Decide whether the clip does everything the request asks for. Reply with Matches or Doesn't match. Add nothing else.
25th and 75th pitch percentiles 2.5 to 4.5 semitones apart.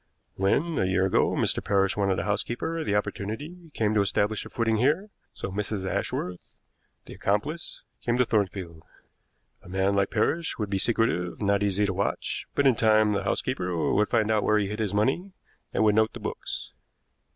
Matches